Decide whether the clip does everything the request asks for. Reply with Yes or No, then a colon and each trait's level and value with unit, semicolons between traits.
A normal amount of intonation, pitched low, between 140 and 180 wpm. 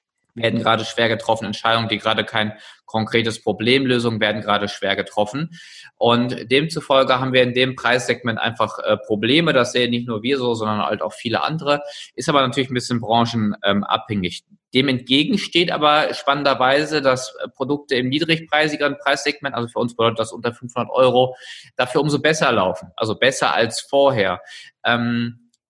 Yes: average, 3.6 semitones; low, 125 Hz; average, 160 wpm